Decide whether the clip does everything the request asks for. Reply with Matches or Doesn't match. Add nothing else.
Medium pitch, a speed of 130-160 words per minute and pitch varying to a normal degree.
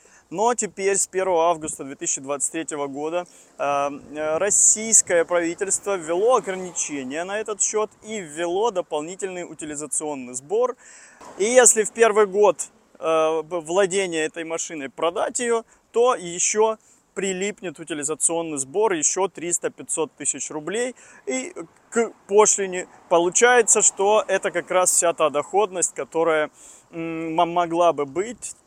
Doesn't match